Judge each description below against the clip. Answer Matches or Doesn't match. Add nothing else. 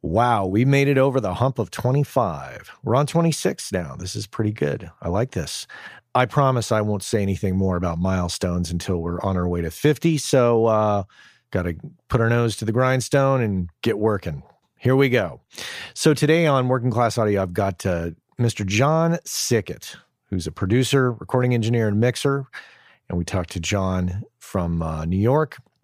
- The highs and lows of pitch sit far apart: Matches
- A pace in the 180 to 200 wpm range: Matches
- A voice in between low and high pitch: Doesn't match